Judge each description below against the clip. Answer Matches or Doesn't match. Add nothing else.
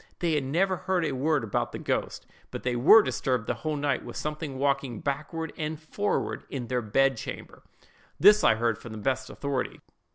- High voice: Doesn't match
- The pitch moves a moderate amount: Matches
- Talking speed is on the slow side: Doesn't match